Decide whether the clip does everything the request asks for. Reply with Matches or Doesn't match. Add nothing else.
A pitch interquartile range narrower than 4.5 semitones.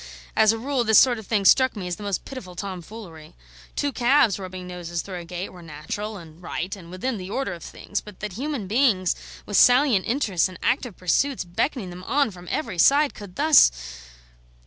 Doesn't match